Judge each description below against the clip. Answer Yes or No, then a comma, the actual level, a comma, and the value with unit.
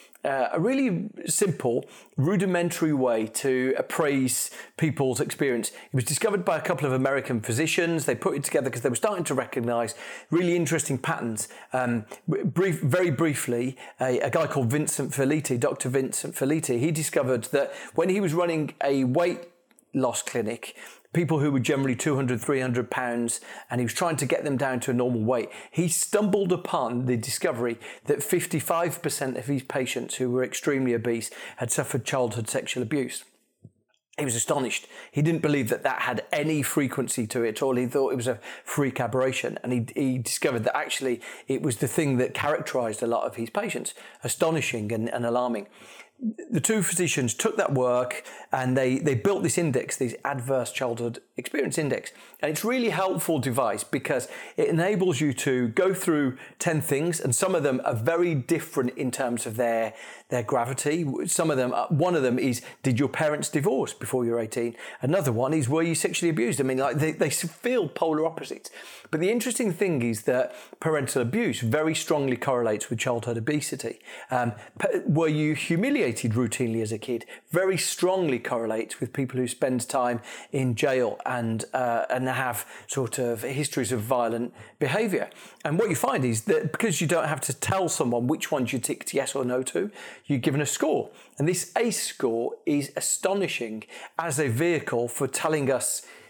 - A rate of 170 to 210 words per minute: Yes, average, 180 wpm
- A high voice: No, low, 135 Hz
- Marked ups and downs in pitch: No, average, 4.8 semitones